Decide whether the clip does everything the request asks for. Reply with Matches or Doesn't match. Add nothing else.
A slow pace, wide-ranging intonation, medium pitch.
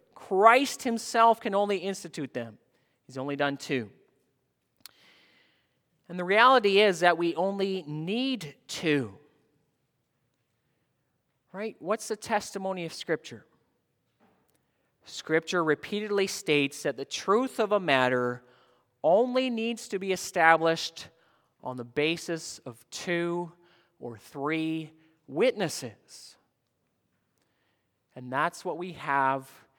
Matches